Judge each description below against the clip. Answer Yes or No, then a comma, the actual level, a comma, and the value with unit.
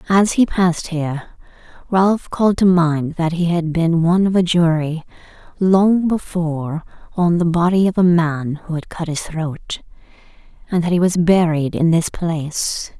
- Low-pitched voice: No, medium, 170 Hz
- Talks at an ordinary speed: Yes, average, 170 wpm